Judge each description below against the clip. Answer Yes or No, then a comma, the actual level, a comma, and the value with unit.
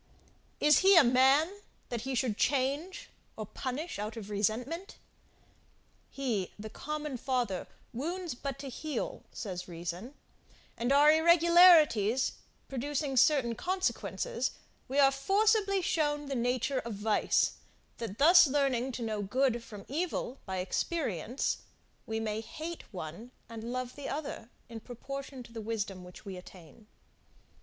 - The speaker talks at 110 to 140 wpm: Yes, slow, 135 wpm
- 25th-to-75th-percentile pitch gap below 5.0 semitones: No, average, 5.3 semitones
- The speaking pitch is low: No, very high, 255 Hz